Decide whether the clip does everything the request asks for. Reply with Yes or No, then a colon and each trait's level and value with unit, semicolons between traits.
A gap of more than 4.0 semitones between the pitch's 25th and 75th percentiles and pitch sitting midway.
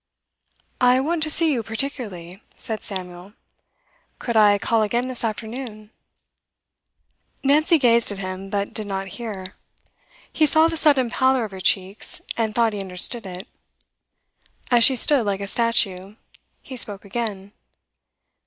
No: average, 4.4 semitones; high, 220 Hz